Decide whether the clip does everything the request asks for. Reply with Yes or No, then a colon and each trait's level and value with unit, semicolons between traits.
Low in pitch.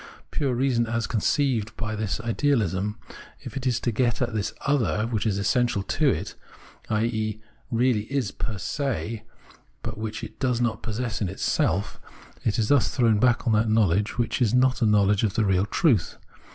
Yes: low, 115 Hz